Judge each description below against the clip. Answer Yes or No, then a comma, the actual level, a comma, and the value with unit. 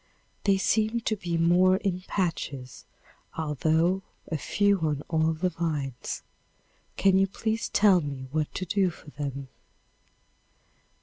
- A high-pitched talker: No, medium, 170 Hz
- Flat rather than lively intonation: No, average, 4.3 semitones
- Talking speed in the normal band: No, slow, 130 wpm